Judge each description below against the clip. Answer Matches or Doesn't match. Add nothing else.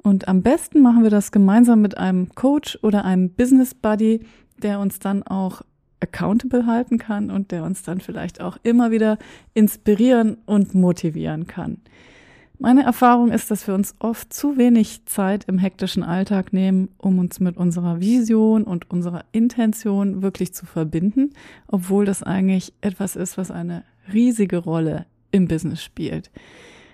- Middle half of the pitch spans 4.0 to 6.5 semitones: Doesn't match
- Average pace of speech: Matches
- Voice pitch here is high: Matches